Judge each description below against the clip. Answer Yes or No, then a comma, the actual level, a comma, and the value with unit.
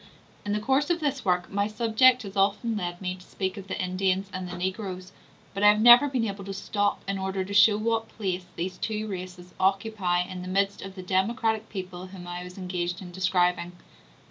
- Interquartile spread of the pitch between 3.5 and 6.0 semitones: No, narrow, 2.6 semitones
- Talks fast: Yes, fast, 215 wpm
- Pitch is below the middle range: No, high, 195 Hz